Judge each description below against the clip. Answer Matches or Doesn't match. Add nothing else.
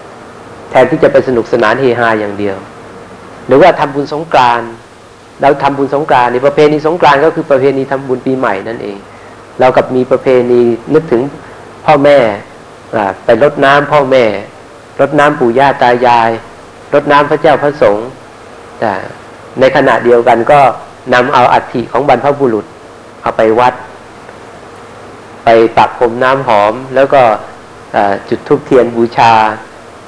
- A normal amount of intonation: Matches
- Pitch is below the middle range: Matches